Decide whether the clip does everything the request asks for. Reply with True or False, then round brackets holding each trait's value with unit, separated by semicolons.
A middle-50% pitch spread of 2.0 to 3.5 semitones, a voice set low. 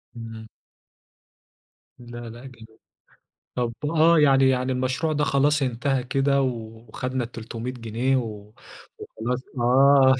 True (2.8 semitones; 125 Hz)